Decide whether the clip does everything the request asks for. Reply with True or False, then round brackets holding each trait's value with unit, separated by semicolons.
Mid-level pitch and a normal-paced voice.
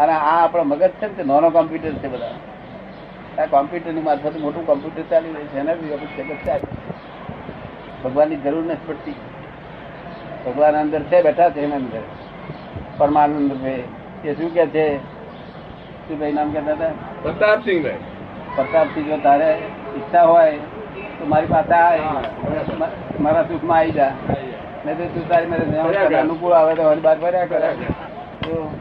True (155 Hz; 100 wpm)